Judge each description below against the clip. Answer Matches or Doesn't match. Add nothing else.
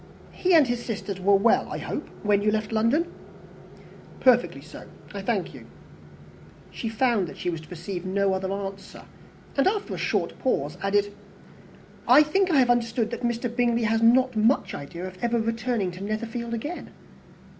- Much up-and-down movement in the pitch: Doesn't match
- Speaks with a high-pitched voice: Matches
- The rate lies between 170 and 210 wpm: Matches